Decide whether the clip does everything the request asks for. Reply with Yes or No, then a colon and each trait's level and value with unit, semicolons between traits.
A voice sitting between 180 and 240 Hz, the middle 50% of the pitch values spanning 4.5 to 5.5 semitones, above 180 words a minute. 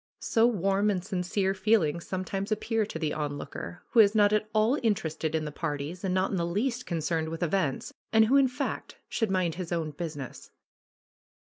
Yes: medium, 185 Hz; average, 4.8 semitones; average, 200 wpm